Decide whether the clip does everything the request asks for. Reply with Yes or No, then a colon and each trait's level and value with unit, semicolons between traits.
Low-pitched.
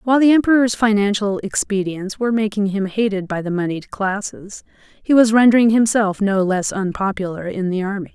No: high, 205 Hz